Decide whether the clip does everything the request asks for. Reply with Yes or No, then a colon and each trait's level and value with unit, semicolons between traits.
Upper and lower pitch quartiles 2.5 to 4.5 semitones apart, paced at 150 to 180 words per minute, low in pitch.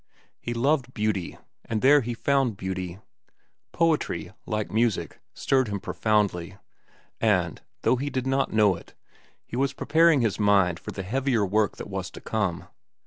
No: average, 5.2 semitones; average, 155 wpm; low, 110 Hz